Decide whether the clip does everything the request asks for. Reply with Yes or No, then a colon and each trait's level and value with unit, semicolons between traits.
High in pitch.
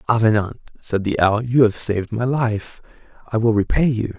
No: low, 110 Hz